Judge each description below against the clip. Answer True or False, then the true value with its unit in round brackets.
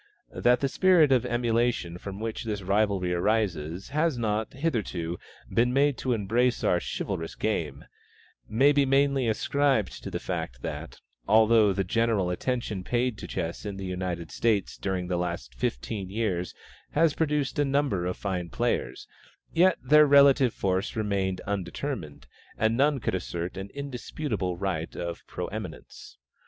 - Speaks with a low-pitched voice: True (110 Hz)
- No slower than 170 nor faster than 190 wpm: False (150 wpm)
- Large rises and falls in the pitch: True (6.2 semitones)